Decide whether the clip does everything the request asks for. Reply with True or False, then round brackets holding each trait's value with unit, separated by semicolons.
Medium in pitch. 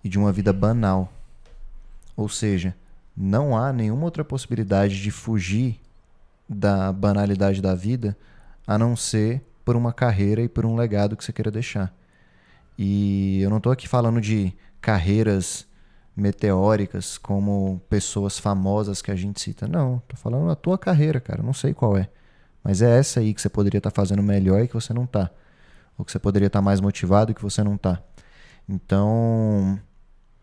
False (105 Hz)